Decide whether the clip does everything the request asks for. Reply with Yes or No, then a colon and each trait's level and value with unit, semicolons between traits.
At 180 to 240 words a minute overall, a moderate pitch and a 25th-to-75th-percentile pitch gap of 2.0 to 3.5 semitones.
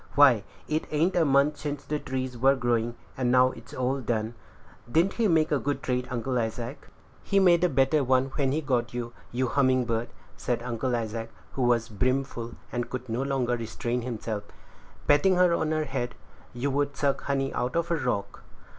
No: average, 200 wpm; low, 130 Hz; average, 3.2 semitones